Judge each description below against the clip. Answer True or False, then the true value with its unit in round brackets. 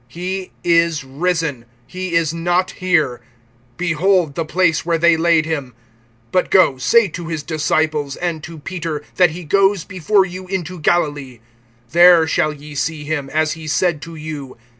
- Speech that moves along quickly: False (160 wpm)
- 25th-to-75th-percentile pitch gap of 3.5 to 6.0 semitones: False (2.9 semitones)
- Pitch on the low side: False (165 Hz)